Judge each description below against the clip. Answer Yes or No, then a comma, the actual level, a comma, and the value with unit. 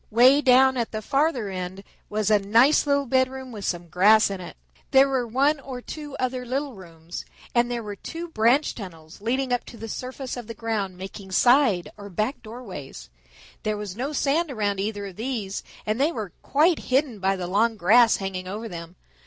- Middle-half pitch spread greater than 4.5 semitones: Yes, average, 5.0 semitones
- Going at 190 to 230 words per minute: Yes, average, 195 wpm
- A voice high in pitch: Yes, high, 225 Hz